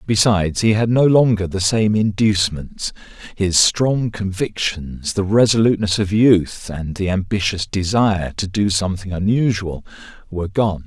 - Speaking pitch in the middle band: No, low, 100 Hz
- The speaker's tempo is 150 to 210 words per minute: No, average, 140 wpm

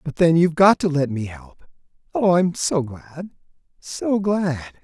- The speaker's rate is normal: Yes, average, 160 wpm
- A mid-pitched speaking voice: Yes, medium, 160 Hz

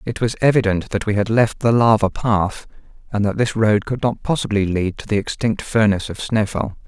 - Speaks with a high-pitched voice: No, low, 110 Hz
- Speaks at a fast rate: Yes, fast, 210 wpm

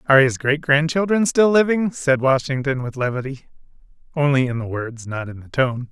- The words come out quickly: No, average, 195 wpm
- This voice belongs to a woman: No, male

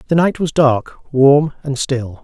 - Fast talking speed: No, average, 190 wpm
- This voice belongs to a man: Yes, male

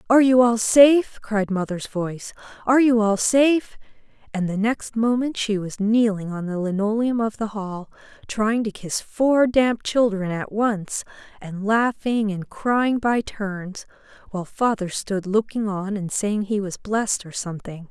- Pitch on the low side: No, high, 215 Hz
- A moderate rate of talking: Yes, average, 170 wpm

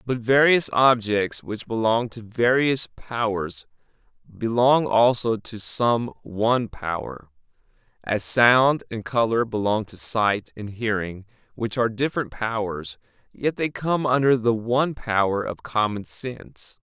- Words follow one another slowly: Yes, slow, 130 wpm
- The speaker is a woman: No, male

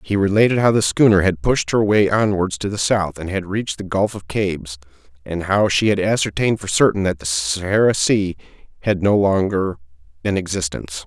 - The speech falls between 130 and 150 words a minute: No, average, 195 wpm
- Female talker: No, male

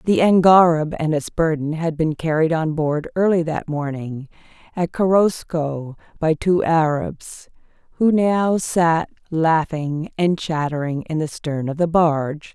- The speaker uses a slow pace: No, average, 145 wpm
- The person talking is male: No, female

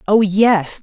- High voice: Yes, high, 200 Hz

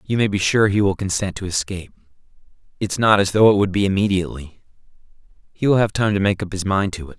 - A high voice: No, low, 100 Hz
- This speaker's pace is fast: Yes, fast, 235 wpm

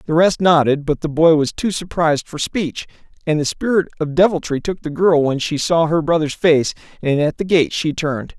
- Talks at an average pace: No, fast, 220 wpm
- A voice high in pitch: No, medium, 160 Hz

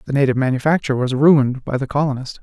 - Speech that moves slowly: No, average, 200 wpm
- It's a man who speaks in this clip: Yes, male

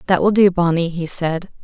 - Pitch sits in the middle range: Yes, medium, 175 Hz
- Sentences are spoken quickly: Yes, fast, 220 wpm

